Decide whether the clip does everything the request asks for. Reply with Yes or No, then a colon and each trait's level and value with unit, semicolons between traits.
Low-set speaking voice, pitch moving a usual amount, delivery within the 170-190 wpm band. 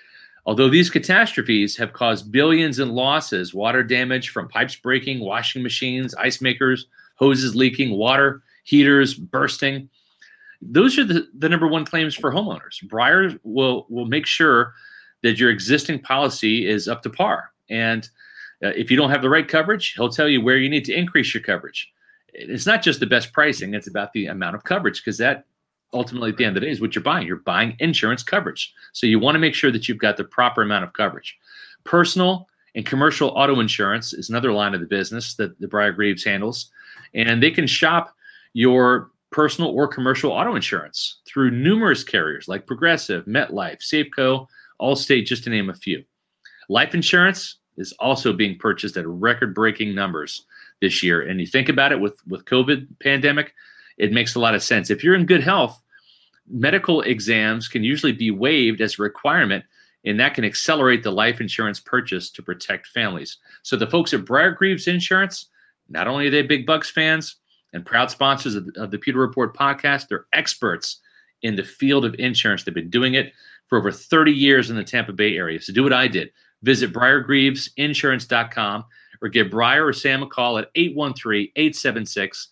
Yes: low, 130 Hz; average, 4.9 semitones; average, 185 wpm